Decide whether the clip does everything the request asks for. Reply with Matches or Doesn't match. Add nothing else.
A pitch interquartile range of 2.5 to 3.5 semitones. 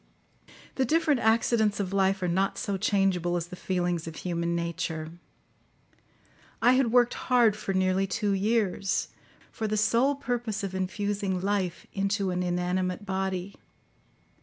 Matches